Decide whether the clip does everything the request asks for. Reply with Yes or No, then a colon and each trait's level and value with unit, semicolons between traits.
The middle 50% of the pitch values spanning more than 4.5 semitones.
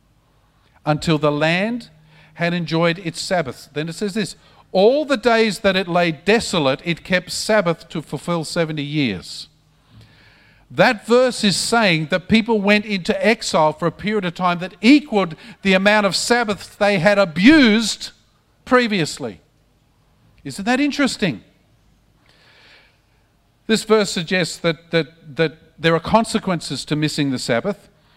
Yes: average, 5.1 semitones